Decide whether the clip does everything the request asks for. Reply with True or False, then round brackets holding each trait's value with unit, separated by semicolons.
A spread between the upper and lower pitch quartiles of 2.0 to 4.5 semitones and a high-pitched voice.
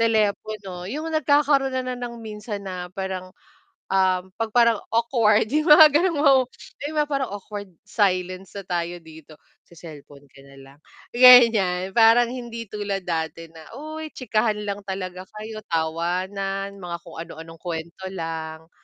False (5.1 semitones; 200 Hz)